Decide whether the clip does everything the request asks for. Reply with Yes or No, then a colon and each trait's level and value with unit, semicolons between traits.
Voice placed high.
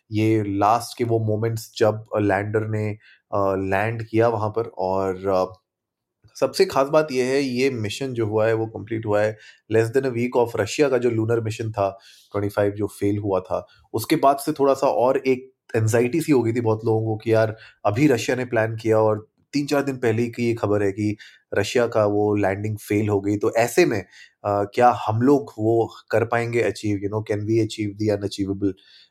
No: low, 110 Hz